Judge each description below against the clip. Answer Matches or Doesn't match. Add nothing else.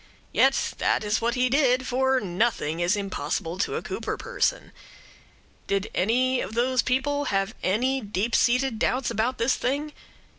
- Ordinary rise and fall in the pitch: Matches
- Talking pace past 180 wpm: Doesn't match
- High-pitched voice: Matches